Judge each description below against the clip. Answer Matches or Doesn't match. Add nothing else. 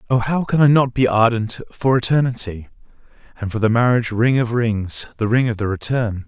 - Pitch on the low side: Matches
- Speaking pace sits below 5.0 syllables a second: Doesn't match